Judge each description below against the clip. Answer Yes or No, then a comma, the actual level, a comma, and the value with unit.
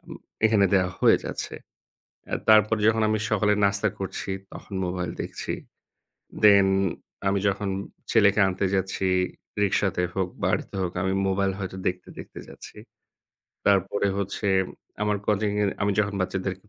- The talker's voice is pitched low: Yes, low, 100 Hz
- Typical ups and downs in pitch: No, narrow, 1.6 semitones